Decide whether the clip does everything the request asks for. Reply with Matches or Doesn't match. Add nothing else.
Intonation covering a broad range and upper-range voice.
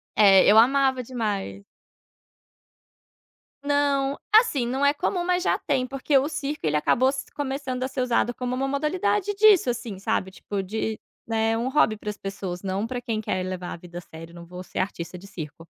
Matches